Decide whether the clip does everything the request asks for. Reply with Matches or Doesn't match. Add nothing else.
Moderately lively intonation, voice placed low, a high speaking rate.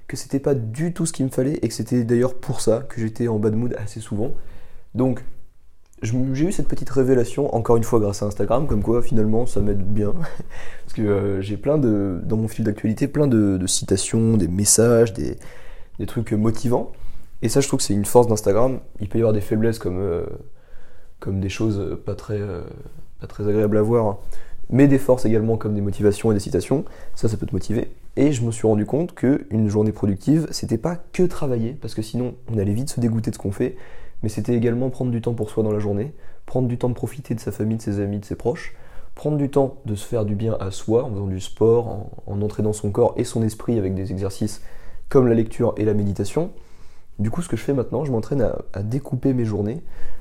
Matches